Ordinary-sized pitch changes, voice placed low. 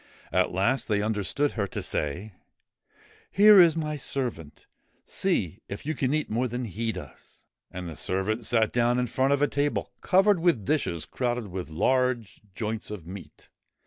No: wide, 6.3 semitones; low, 115 Hz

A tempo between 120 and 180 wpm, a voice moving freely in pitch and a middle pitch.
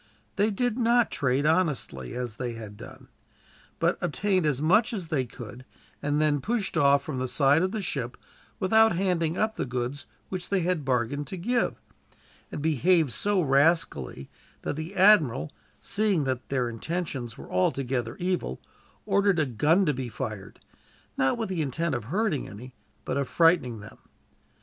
Yes: average, 165 wpm; wide, 6.6 semitones; medium, 150 Hz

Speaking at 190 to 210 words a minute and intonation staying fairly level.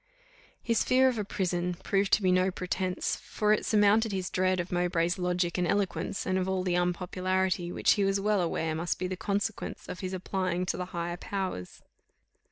Yes: average, 195 wpm; narrow, 1.8 semitones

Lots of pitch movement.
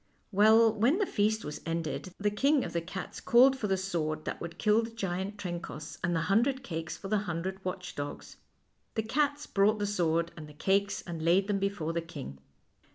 No: average, 4.4 semitones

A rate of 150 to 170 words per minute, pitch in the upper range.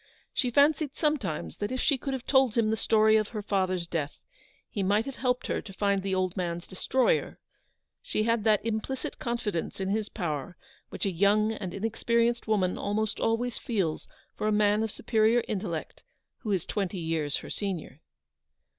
No: average, 180 wpm; high, 210 Hz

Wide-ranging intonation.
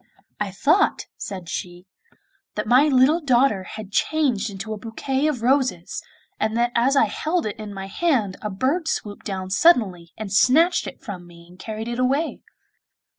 Yes: wide, 5.8 semitones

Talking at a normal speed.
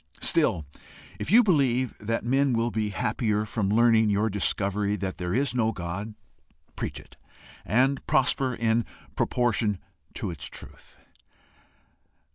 No: slow, 130 wpm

